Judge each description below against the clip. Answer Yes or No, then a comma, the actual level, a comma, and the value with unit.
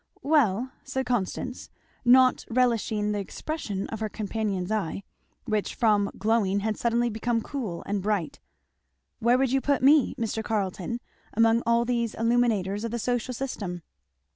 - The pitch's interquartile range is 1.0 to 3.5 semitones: Yes, average, 3.0 semitones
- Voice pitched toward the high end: Yes, high, 225 Hz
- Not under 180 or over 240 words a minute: No, average, 145 wpm